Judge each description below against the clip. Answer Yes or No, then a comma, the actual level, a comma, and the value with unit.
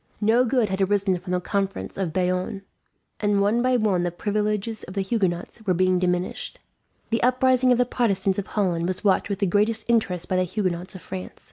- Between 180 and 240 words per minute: Yes, fast, 205 wpm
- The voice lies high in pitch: Yes, high, 195 Hz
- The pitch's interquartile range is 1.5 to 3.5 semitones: Yes, average, 3.1 semitones